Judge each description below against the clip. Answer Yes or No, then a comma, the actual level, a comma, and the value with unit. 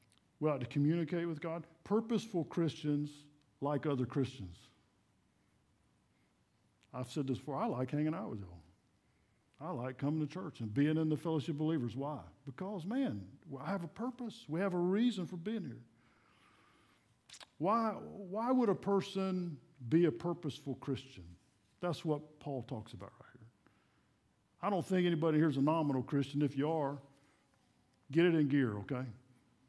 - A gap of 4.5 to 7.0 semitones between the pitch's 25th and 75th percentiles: Yes, average, 5.1 semitones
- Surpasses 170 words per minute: No, average, 160 wpm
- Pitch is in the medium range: Yes, medium, 145 Hz